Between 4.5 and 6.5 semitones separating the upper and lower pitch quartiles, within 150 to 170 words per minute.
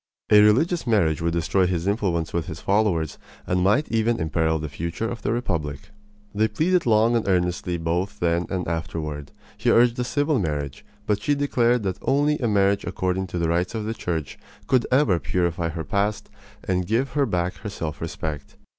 No: wide, 5.4 semitones; average, 190 wpm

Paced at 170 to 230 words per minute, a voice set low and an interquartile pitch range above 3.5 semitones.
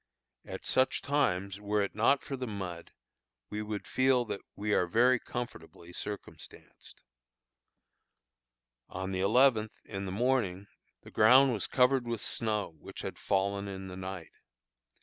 No: average, 145 wpm; low, 105 Hz; average, 4.4 semitones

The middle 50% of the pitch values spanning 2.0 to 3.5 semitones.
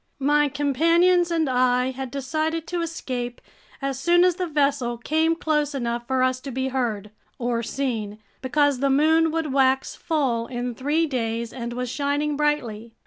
No: average, 3.9 semitones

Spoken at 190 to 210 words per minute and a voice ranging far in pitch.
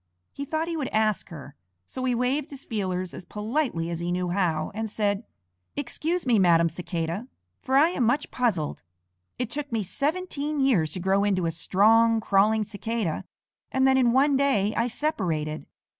No: average, 175 wpm; wide, 6.7 semitones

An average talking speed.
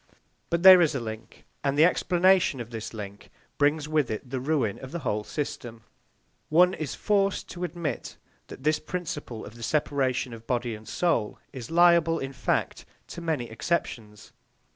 Yes: average, 170 wpm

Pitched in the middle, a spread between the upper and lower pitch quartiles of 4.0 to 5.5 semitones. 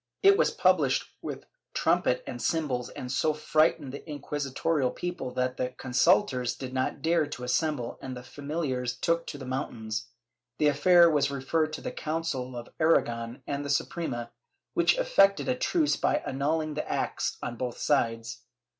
Yes: medium, 145 Hz; average, 4.3 semitones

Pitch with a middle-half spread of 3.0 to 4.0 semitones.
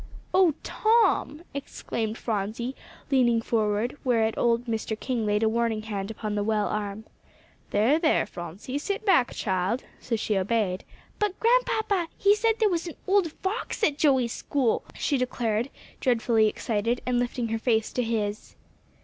No: average, 5.1 semitones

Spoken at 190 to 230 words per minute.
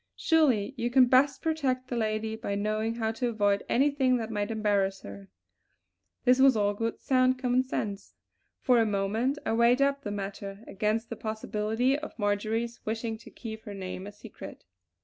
No: average, 175 wpm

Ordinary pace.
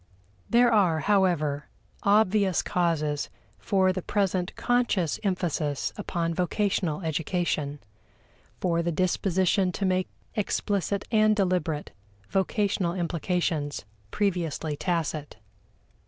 No: slow, 95 wpm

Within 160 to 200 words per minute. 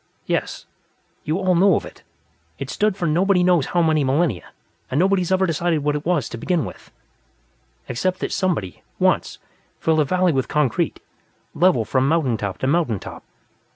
Yes: average, 175 wpm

